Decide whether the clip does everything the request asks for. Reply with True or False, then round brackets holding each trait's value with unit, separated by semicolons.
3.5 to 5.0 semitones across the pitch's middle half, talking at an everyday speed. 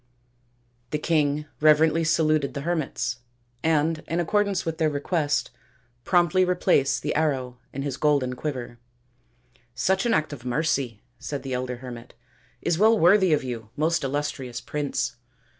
True (4.1 semitones; 150 wpm)